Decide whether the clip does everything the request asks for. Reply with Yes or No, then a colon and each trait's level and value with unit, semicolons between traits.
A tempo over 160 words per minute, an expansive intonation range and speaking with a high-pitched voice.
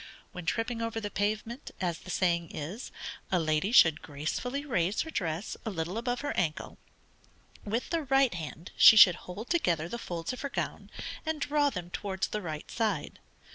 Yes: average, 180 wpm; wide, 6.3 semitones; high, 205 Hz